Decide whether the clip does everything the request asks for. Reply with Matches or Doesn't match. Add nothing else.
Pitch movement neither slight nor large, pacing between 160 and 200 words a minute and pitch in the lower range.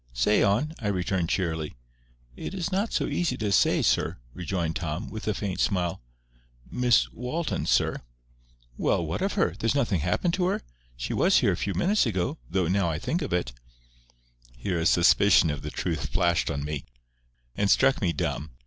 Doesn't match